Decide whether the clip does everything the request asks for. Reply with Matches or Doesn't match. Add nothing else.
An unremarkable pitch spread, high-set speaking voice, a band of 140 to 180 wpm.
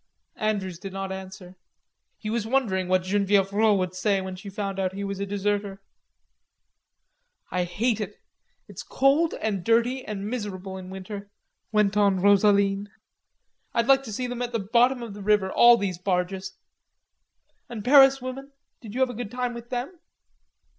Matches